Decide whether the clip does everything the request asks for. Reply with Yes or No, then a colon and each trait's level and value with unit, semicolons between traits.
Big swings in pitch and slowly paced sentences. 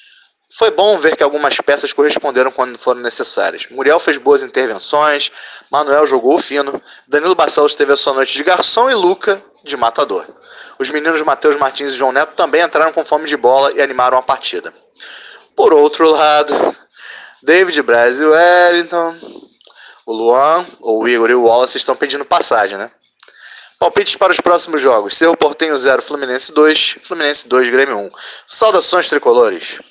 No: wide, 6.0 semitones; average, 160 wpm